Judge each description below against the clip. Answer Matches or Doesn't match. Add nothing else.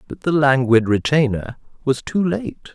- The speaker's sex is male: Matches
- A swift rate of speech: Doesn't match